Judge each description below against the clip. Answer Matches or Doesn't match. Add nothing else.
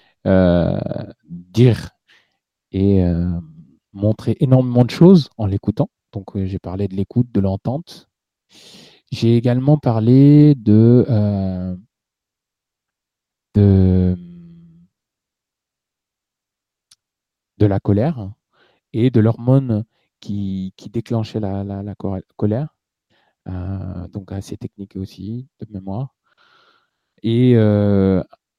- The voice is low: Matches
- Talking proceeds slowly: Matches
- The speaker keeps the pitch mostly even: Doesn't match